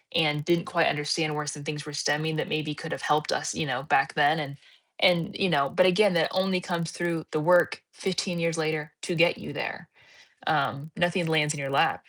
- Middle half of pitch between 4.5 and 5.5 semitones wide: No, narrow, 2.5 semitones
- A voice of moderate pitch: Yes, medium, 160 Hz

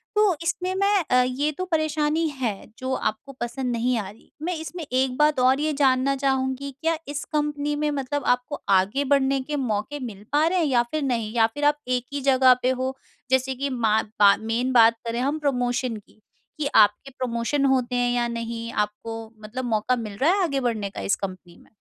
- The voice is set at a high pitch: Yes, very high, 260 Hz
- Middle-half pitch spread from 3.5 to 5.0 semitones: Yes, average, 3.9 semitones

